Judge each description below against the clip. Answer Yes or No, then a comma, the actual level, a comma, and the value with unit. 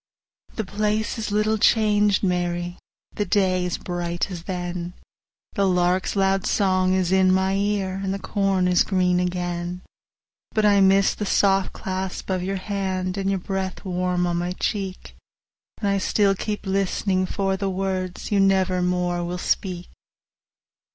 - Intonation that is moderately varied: No, narrow, 1.6 semitones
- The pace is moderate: Yes, average, 165 wpm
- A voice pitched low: No, high, 190 Hz